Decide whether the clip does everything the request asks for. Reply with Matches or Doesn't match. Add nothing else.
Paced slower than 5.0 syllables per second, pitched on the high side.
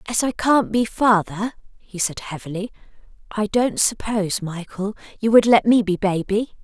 Matches